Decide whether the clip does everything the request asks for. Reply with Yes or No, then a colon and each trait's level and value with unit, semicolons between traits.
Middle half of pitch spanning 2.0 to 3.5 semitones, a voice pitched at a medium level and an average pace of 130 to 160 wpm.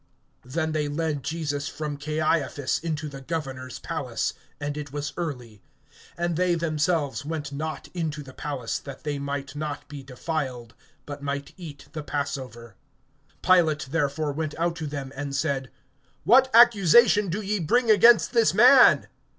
Yes: average, 2.9 semitones; medium, 150 Hz; average, 150 wpm